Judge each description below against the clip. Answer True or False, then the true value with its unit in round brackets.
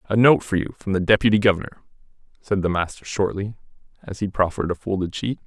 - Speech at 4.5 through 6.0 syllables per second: False (6.6 syllables/s)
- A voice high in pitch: False (100 Hz)